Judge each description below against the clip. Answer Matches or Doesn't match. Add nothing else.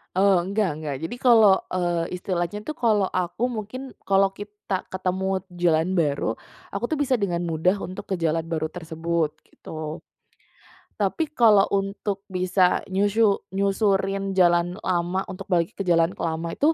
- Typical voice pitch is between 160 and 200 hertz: Matches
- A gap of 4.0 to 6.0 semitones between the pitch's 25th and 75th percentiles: Doesn't match